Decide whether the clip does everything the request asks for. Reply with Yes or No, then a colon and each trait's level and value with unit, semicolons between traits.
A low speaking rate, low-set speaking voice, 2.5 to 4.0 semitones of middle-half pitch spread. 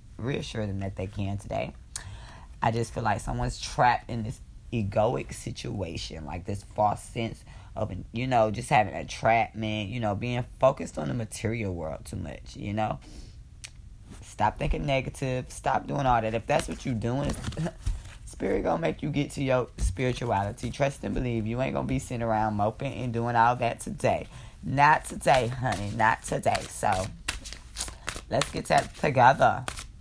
No: average, 170 wpm; low, 110 Hz; average, 3.4 semitones